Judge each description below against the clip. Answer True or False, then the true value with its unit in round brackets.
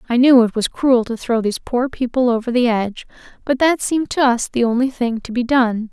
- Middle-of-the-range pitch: False (245 Hz)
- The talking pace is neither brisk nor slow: False (245 wpm)